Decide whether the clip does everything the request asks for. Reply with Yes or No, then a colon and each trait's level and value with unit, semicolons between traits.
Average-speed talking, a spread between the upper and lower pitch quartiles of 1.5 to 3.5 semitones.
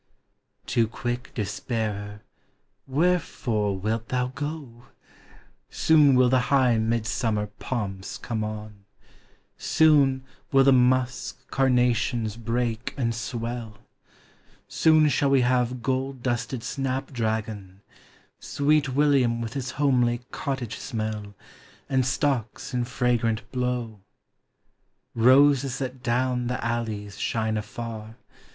No: slow, 105 wpm; average, 2.9 semitones